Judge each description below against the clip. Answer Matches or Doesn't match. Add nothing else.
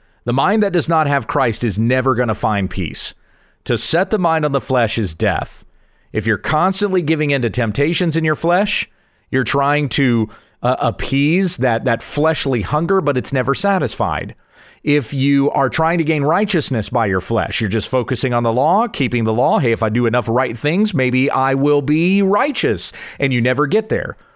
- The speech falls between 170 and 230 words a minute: Matches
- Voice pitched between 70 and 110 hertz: Doesn't match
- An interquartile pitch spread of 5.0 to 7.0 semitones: Matches